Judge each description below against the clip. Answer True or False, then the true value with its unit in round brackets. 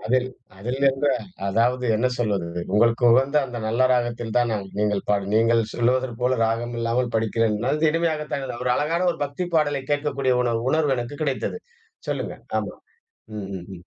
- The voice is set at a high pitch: False (125 Hz)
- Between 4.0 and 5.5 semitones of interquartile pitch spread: False (3.4 semitones)